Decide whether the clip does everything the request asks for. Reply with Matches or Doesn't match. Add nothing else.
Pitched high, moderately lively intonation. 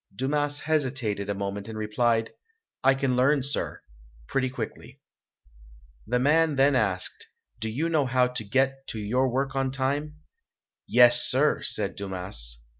Doesn't match